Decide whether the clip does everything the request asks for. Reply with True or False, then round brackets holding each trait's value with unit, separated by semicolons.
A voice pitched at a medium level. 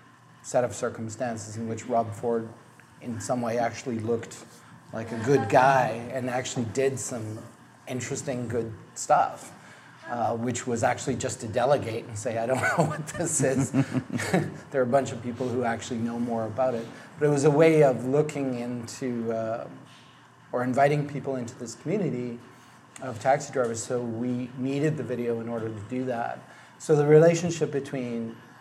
False (125 Hz)